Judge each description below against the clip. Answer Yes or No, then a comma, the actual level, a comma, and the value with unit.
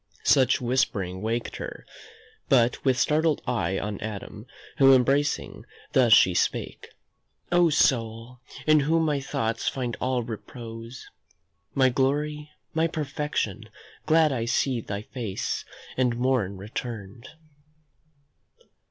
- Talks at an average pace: No, slow, 115 wpm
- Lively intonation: No, average, 3.8 semitones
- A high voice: No, low, 125 Hz